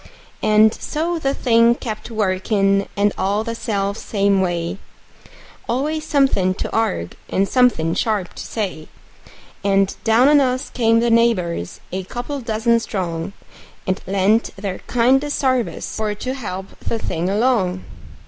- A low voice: No, high, 215 Hz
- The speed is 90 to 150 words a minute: Yes, average, 140 wpm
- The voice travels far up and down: No, average, 4.0 semitones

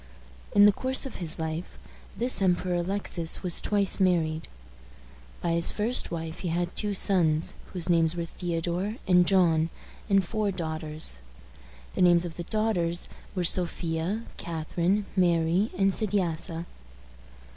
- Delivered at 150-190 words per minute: No, slow, 135 wpm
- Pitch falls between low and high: Yes, medium, 175 Hz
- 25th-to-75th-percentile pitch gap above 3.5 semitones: No, average, 2.9 semitones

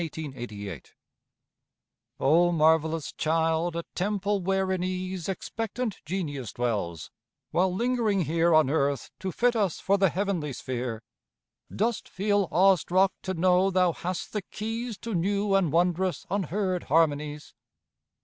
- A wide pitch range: No, average, 3.7 semitones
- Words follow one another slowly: Yes, slow, 130 wpm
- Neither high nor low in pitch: Yes, medium, 180 Hz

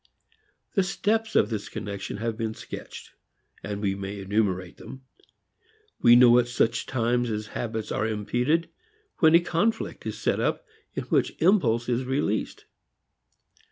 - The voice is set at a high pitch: No, low, 115 Hz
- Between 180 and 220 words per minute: No, average, 145 wpm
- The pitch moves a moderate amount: Yes, average, 4.0 semitones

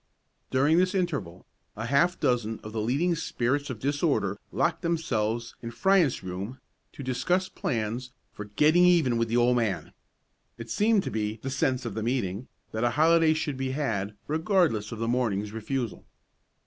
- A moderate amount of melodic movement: No, wide, 5.9 semitones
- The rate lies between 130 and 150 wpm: No, average, 170 wpm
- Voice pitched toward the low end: Yes, low, 125 Hz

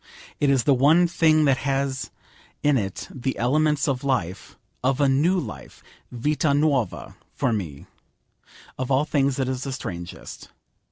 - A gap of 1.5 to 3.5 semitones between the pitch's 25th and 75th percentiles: Yes, average, 2.7 semitones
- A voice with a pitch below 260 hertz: Yes, low, 135 Hz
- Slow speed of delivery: No, average, 155 wpm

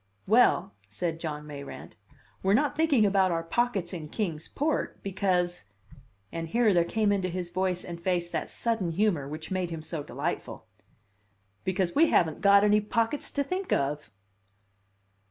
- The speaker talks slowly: No, average, 155 wpm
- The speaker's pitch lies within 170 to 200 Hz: Yes, medium, 185 Hz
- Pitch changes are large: No, average, 4.3 semitones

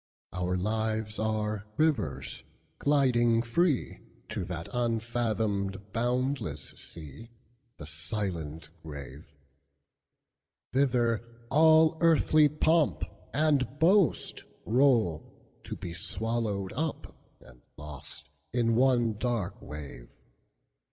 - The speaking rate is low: Yes, slow, 75 wpm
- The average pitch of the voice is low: Yes, low, 110 Hz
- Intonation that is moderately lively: No, wide, 7.1 semitones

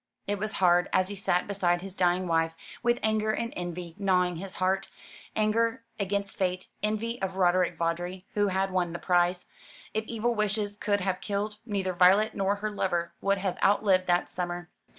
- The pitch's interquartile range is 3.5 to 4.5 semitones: No, narrow, 2.5 semitones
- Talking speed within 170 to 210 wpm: Yes, average, 180 wpm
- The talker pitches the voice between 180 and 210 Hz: Yes, high, 190 Hz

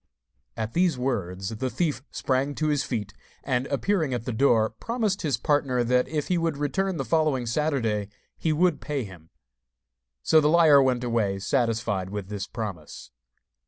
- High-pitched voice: No, low, 130 Hz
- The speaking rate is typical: Yes, average, 165 wpm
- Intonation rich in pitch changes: Yes, wide, 5.7 semitones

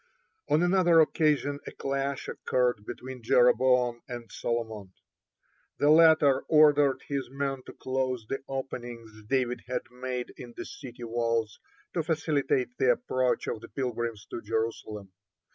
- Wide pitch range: No, average, 2.9 semitones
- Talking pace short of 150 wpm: Yes, average, 140 wpm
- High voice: No, low, 130 Hz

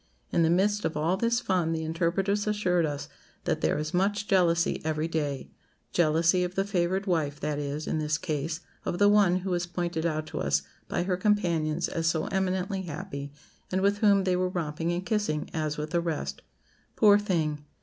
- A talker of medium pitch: Yes, medium, 175 Hz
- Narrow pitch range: No, average, 3.6 semitones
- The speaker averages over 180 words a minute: Yes, average, 195 wpm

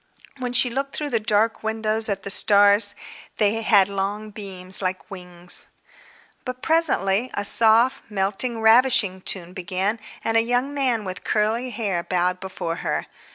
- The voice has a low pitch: No, high, 210 Hz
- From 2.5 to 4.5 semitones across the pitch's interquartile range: Yes, average, 3.5 semitones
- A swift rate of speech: No, average, 155 wpm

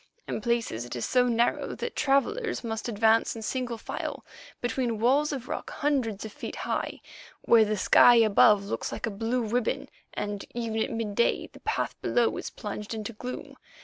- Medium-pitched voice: No, high, 230 Hz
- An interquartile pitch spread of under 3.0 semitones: Yes, narrow, 2.4 semitones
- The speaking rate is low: No, average, 180 wpm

